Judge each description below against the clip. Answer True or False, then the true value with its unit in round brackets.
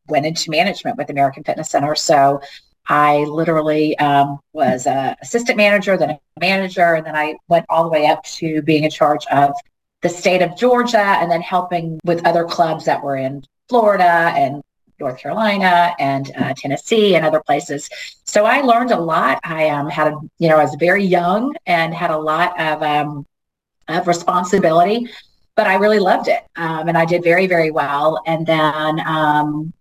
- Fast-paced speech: False (185 wpm)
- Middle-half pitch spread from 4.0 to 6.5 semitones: False (3.0 semitones)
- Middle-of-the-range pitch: True (165 Hz)